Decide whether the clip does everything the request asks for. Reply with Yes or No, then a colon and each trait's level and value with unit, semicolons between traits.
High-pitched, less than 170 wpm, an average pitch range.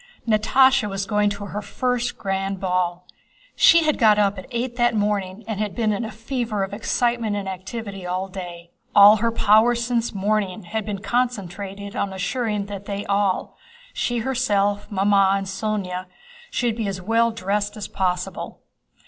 Yes: high, 205 Hz; average, 160 wpm; average, 3.1 semitones